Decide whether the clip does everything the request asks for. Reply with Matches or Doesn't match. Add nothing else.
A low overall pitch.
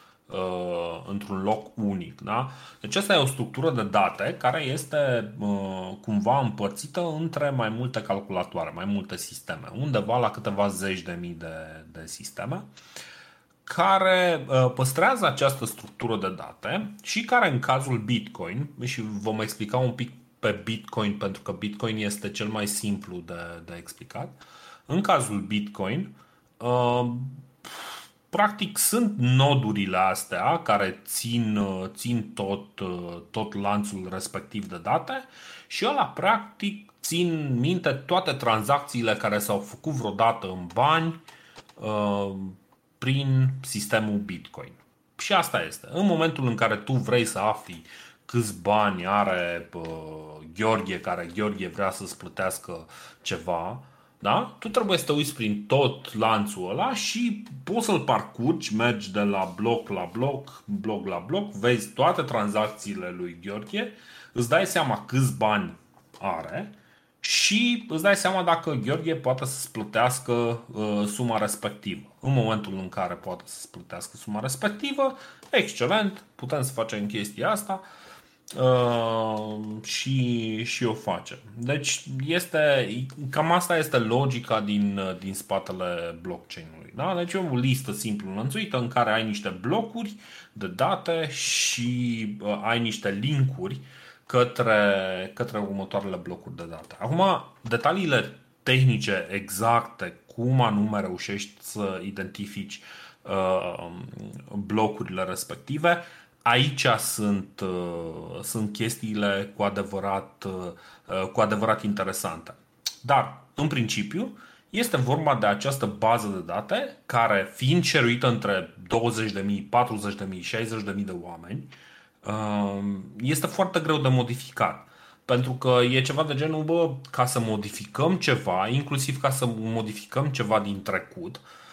Matches